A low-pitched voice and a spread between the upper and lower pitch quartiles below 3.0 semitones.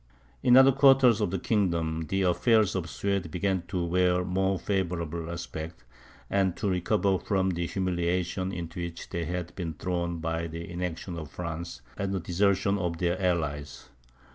Yes: very low, 90 Hz; narrow, 2.4 semitones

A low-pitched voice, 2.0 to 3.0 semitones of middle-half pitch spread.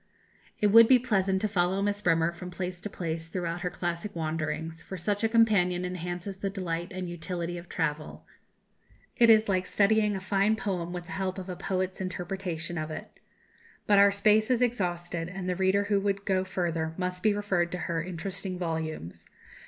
No: medium, 185 Hz; average, 2.7 semitones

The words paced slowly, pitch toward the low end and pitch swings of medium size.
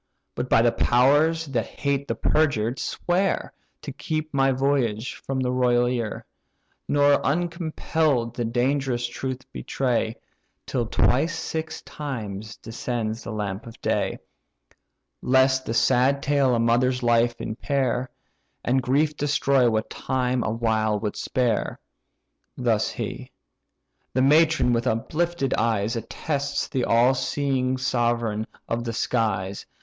Yes: slow, 125 wpm; low, 125 Hz; average, 3.3 semitones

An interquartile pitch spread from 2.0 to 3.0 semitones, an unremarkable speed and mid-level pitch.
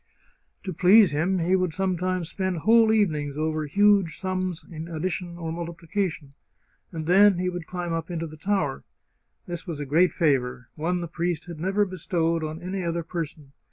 Yes: average, 2.7 semitones; average, 180 wpm; medium, 175 Hz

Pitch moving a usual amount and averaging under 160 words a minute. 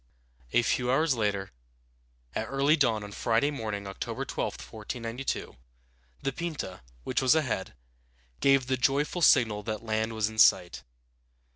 Yes: average, 4.3 semitones; average, 140 wpm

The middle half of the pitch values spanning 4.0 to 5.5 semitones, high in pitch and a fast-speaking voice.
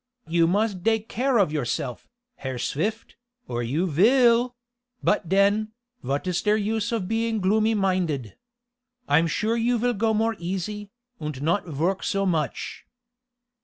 No: average, 5.2 semitones; high, 195 Hz; average, 150 wpm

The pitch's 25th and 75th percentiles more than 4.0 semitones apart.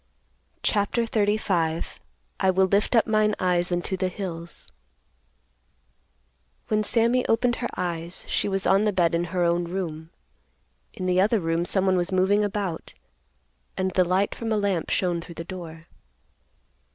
No: average, 3.0 semitones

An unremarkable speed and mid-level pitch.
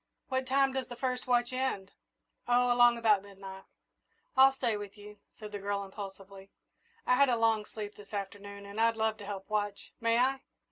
No: average, 190 wpm; high, 215 Hz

